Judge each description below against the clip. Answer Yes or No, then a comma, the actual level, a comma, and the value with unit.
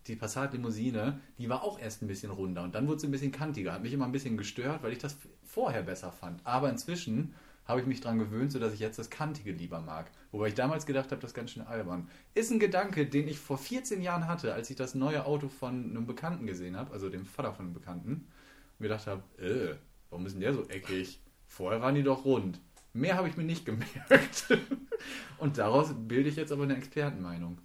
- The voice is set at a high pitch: No, low, 130 Hz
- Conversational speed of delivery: No, fast, 230 wpm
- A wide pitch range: Yes, wide, 5.7 semitones